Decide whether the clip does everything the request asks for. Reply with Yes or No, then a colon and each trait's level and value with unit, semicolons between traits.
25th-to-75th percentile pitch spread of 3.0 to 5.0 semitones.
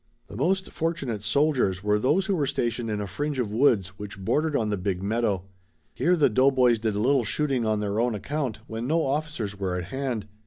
No: wide, 5.5 semitones